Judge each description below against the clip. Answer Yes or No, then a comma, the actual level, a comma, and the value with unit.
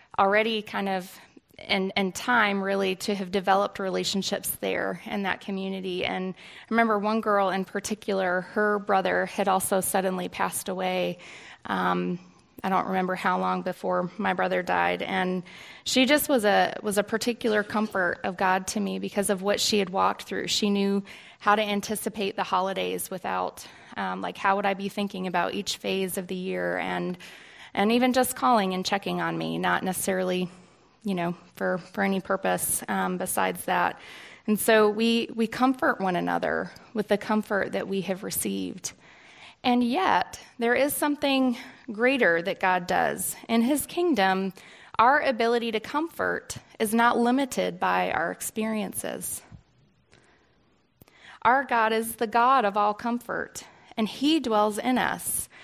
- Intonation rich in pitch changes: No, average, 3.2 semitones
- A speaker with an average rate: Yes, average, 160 wpm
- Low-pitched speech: No, high, 200 Hz